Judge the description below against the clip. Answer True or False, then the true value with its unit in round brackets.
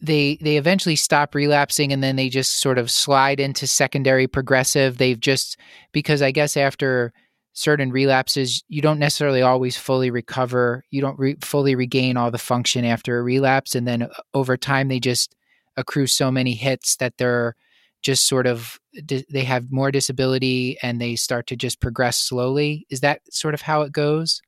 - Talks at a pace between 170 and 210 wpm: True (180 wpm)